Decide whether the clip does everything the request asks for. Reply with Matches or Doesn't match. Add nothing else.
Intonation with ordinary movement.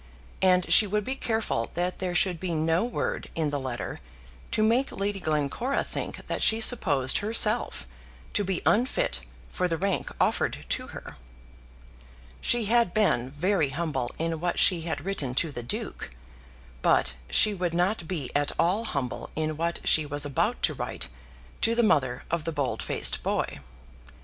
Doesn't match